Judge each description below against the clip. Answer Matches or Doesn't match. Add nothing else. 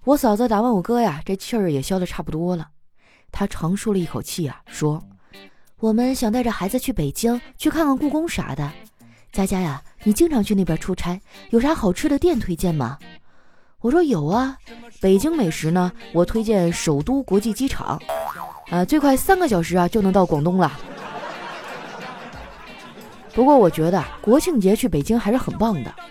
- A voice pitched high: Matches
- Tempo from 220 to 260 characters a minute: Matches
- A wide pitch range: Matches